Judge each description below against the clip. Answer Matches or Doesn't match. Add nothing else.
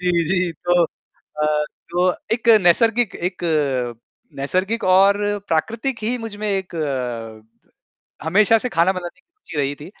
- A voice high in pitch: Doesn't match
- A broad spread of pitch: Matches